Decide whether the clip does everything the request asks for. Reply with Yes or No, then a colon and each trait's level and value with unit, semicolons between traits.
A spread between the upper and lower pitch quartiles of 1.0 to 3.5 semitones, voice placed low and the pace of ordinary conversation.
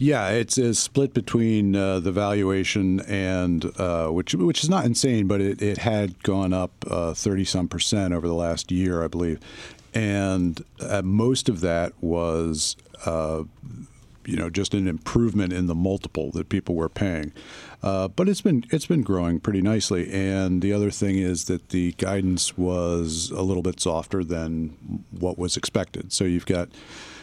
Yes: average, 3.0 semitones; very low, 95 Hz; average, 170 wpm